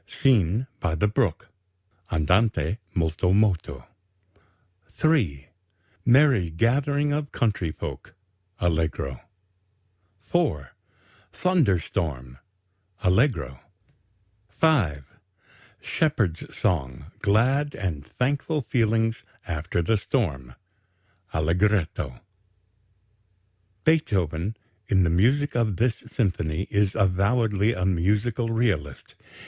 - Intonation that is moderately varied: No, wide, 6.6 semitones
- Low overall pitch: Yes, low, 100 Hz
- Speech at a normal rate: No, slow, 85 wpm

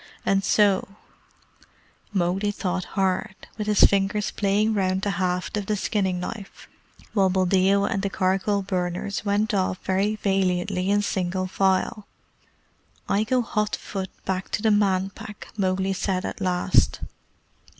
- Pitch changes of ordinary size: No, narrow, 1.7 semitones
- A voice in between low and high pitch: No, high, 195 Hz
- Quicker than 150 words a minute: No, average, 145 wpm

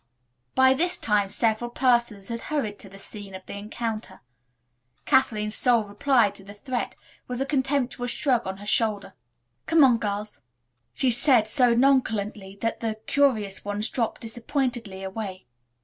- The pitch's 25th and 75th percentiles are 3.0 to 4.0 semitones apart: Yes, average, 3.7 semitones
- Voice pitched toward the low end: No, high, 225 Hz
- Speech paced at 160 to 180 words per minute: No, average, 150 wpm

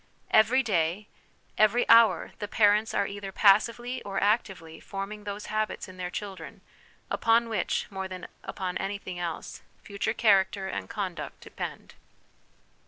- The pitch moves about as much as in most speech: No, narrow, 2.3 semitones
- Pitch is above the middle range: Yes, high, 200 Hz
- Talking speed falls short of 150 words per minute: Yes, slow, 135 wpm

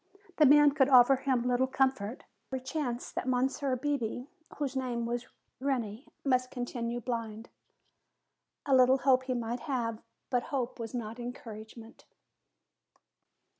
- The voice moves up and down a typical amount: No, narrow, 2.1 semitones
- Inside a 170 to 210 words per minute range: No, average, 140 wpm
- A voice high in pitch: Yes, very high, 250 Hz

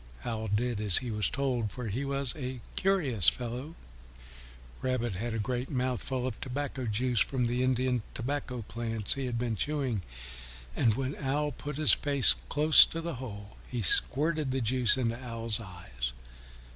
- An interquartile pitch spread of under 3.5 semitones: Yes, average, 3.1 semitones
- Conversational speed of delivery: Yes, average, 165 wpm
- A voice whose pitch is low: Yes, low, 125 Hz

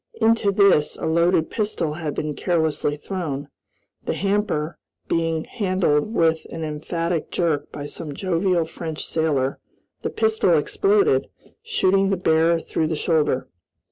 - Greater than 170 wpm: No, slow, 135 wpm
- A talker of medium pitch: Yes, medium, 165 Hz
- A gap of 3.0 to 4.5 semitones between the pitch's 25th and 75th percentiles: Yes, average, 3.8 semitones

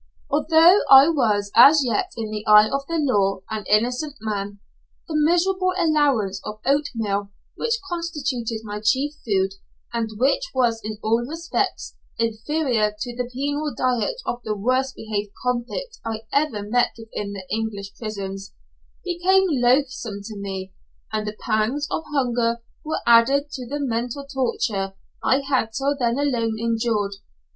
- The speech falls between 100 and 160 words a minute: Yes, average, 150 wpm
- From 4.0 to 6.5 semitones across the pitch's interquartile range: Yes, average, 5.0 semitones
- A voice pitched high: Yes, high, 240 Hz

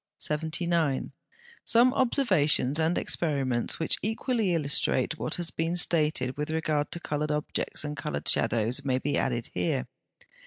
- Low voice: No, medium, 150 Hz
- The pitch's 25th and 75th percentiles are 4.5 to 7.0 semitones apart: No, average, 3.9 semitones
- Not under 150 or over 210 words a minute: No, average, 140 wpm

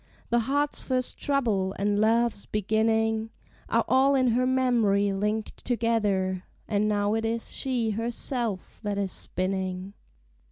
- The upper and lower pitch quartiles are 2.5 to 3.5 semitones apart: Yes, average, 2.9 semitones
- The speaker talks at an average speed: No, slow, 130 wpm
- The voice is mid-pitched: No, high, 220 Hz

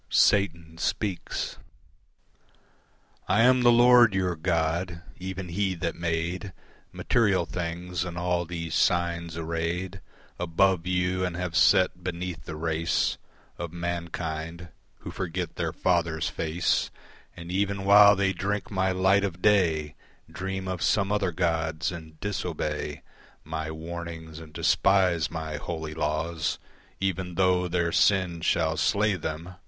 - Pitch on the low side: Yes, very low, 85 Hz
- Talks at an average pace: No, slow, 130 wpm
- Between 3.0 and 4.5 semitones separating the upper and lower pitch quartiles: No, narrow, 2.4 semitones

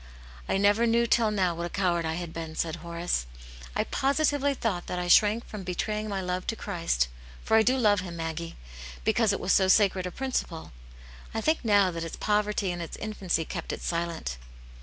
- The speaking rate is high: Yes, fast, 220 wpm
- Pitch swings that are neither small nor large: Yes, average, 4.2 semitones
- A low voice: No, medium, 185 Hz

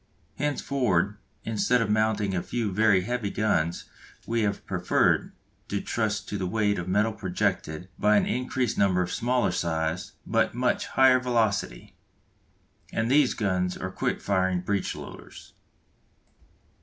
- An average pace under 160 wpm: Yes, average, 145 wpm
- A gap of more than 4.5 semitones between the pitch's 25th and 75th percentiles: No, average, 3.8 semitones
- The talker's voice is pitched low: Yes, low, 105 Hz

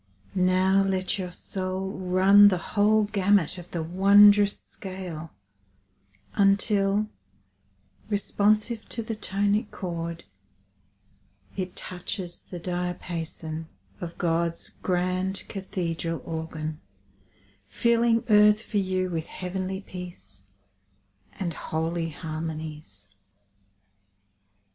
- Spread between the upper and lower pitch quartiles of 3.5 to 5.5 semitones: No, average, 3.1 semitones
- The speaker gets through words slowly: Yes, slow, 90 wpm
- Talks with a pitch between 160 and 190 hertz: Yes, medium, 185 Hz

